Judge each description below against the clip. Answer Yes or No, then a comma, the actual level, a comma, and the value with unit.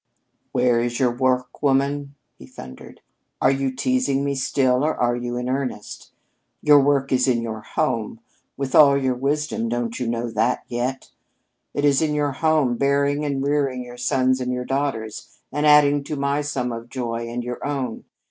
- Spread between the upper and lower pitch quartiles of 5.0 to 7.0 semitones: No, average, 2.7 semitones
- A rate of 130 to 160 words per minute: No, average, 180 wpm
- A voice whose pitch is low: Yes, low, 130 Hz